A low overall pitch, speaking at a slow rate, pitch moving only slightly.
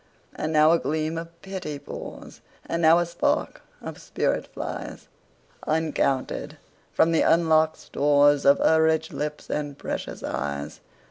No: medium, 155 Hz; slow, 125 wpm; narrow, 2.0 semitones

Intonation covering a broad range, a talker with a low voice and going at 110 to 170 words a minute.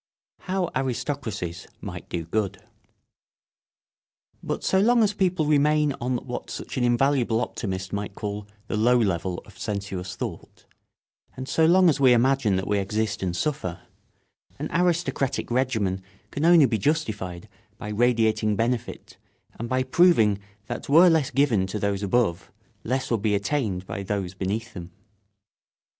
Yes: wide, 6.0 semitones; low, 115 Hz; average, 150 wpm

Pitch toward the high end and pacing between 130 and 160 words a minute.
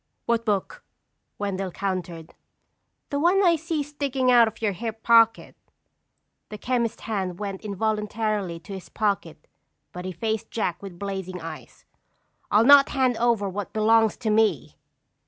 Yes: high, 215 Hz; average, 145 wpm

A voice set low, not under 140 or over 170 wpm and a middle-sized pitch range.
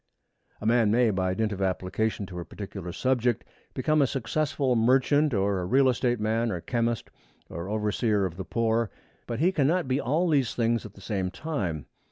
No: low, 115 Hz; average, 185 wpm; average, 4.7 semitones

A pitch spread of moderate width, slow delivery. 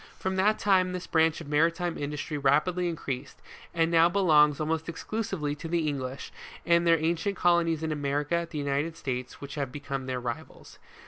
No: average, 3.0 semitones; average, 180 wpm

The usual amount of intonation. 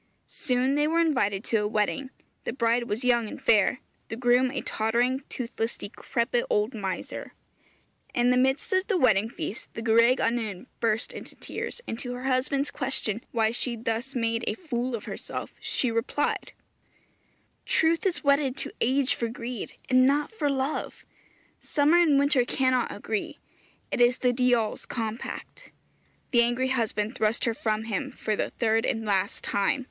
Yes: average, 3.0 semitones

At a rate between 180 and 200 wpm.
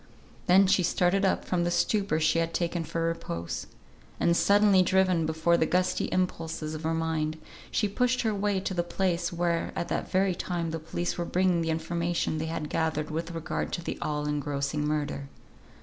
Yes: average, 190 wpm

